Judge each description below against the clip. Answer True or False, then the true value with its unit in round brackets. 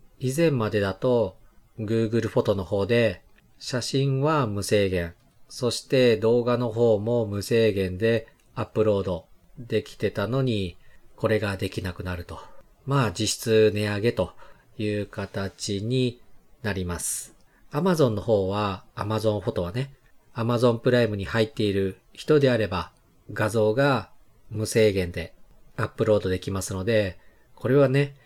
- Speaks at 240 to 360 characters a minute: True (295 characters per minute)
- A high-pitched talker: False (110 Hz)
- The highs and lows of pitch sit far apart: False (3.5 semitones)